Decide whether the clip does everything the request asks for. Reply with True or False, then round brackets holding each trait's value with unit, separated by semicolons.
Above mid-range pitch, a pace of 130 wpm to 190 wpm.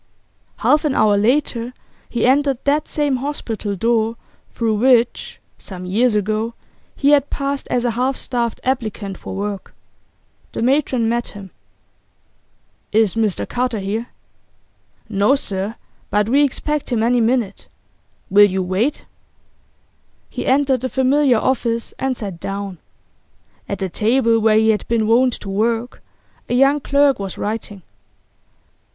True (230 Hz; 140 wpm)